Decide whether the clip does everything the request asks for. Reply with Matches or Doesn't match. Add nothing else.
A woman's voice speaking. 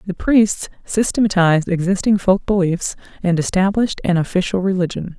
Matches